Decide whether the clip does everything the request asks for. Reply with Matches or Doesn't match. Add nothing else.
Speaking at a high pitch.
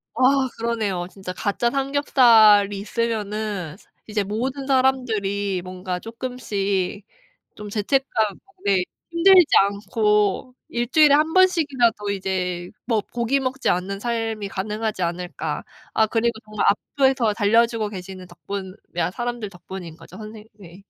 Matches